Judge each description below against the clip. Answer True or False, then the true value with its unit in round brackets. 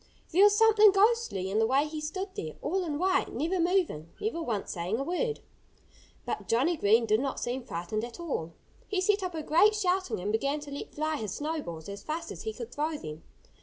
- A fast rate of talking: True (215 wpm)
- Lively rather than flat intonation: True (9.0 semitones)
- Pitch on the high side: True (305 Hz)